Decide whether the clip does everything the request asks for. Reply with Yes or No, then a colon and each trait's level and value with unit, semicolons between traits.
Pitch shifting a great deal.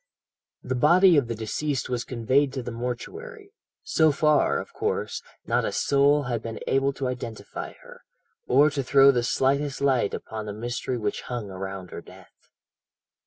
No: average, 3.5 semitones